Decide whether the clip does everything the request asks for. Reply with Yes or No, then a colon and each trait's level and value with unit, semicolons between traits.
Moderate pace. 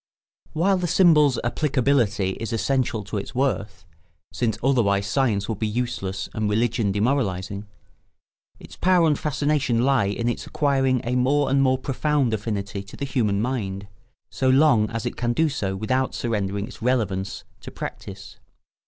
Yes: average, 155 wpm